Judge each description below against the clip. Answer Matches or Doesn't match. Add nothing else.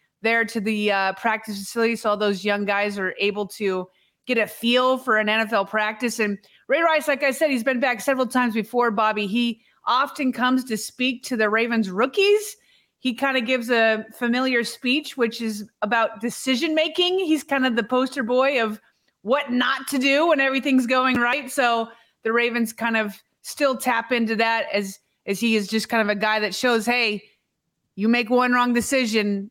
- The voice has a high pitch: Matches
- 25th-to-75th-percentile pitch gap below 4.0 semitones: Matches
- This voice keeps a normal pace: Matches